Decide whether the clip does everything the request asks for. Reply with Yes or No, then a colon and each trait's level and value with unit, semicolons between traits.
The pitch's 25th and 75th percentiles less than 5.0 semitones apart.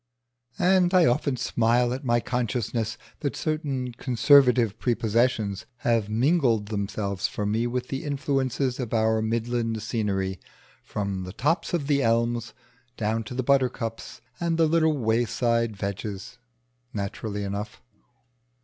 Yes: average, 3.3 semitones